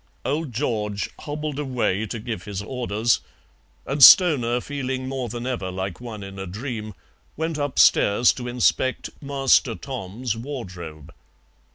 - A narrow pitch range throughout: No, average, 4.5 semitones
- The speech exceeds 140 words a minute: No, slow, 135 wpm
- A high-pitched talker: No, low, 120 Hz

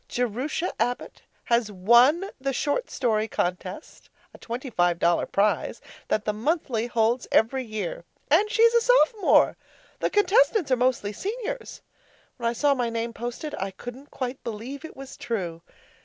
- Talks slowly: No, average, 155 wpm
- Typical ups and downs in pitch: No, wide, 5.7 semitones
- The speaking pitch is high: Yes, high, 245 Hz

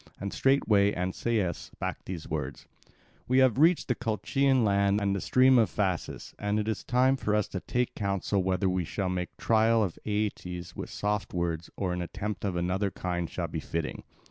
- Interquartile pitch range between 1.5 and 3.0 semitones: No, average, 3.7 semitones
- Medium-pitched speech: No, low, 100 Hz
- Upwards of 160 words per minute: Yes, average, 190 wpm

